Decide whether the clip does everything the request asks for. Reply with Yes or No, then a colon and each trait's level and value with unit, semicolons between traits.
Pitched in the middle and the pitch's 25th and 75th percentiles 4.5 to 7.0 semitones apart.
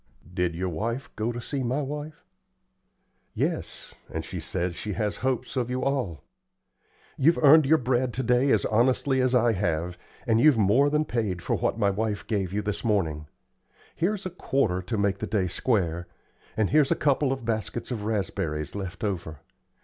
No: low, 115 Hz; wide, 5.5 semitones